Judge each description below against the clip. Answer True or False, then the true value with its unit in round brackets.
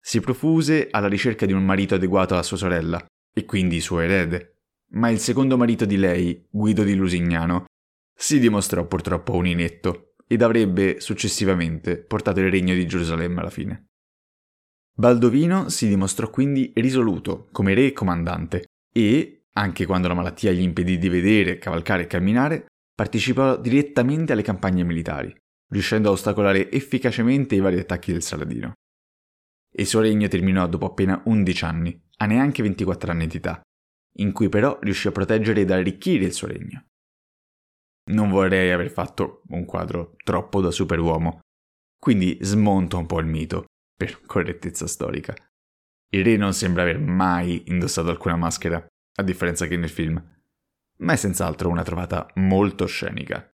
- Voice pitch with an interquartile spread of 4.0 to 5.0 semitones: False (3.4 semitones)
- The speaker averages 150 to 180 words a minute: True (155 wpm)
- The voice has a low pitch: True (95 Hz)